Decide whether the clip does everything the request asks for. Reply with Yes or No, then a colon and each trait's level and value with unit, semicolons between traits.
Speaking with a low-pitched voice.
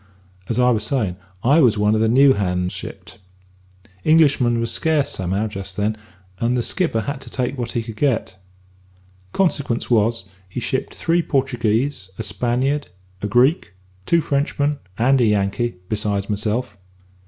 Yes: low, 120 Hz